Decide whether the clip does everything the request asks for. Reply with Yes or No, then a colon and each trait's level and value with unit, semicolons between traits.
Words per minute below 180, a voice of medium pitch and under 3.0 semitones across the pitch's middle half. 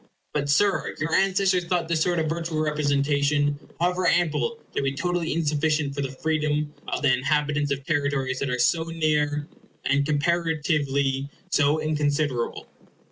Yes: average, 145 wpm; medium, 150 Hz; narrow, 2.4 semitones